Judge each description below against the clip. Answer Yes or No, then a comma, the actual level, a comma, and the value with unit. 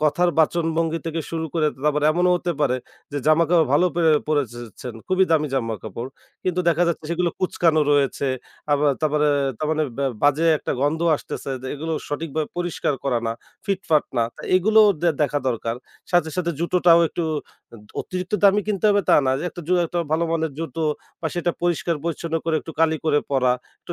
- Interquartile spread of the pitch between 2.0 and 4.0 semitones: Yes, average, 3.0 semitones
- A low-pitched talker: No, medium, 160 Hz